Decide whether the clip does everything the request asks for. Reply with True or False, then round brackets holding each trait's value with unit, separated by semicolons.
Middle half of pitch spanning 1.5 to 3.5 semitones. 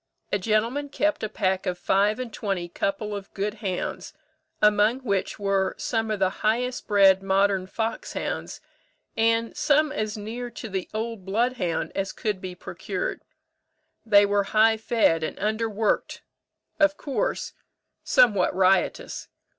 True (2.8 semitones)